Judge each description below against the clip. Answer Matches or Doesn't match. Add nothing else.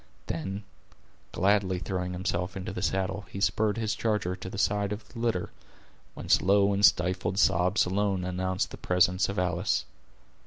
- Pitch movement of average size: Doesn't match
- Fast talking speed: Doesn't match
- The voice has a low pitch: Matches